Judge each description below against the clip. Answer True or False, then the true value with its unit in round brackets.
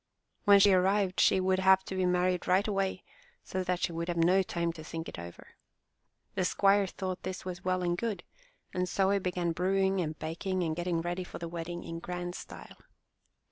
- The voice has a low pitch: False (180 Hz)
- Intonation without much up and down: True (1.7 semitones)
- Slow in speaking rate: False (205 wpm)